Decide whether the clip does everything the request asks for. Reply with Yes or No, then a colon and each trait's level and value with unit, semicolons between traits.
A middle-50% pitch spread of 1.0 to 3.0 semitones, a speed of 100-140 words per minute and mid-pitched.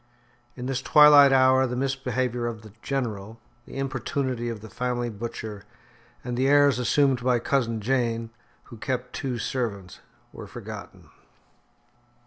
No: narrow, 2.4 semitones; slow, 135 wpm; low, 125 Hz